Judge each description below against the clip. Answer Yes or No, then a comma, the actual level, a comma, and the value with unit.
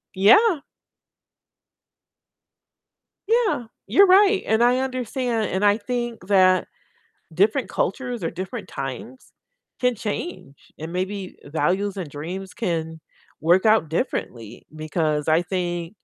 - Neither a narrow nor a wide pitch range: No, wide, 6.3 semitones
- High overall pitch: Yes, high, 195 Hz